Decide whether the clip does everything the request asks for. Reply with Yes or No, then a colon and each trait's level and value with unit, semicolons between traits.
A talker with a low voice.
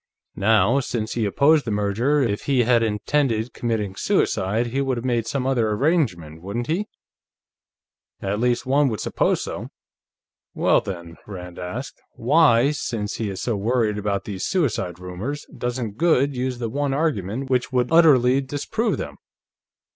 Yes: low, 120 Hz